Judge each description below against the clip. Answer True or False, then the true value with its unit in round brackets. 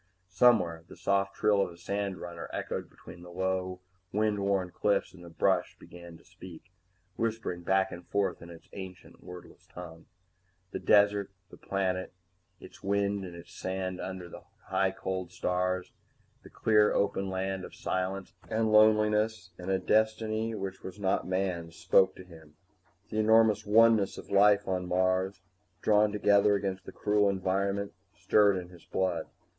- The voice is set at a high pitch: False (95 Hz)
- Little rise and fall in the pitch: True (2.1 semitones)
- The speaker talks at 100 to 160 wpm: True (155 wpm)